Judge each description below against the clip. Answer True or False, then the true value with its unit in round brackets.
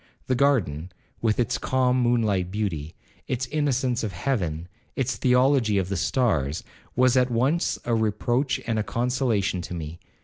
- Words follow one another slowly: False (160 wpm)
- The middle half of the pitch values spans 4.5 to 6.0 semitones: True (5.3 semitones)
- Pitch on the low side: True (115 Hz)